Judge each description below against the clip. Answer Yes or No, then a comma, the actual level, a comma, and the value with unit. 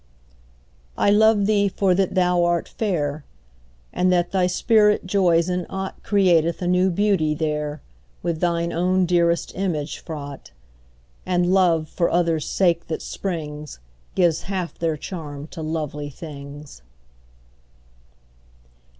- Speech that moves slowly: Yes, slow, 125 wpm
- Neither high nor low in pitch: Yes, medium, 175 Hz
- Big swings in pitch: No, average, 3.0 semitones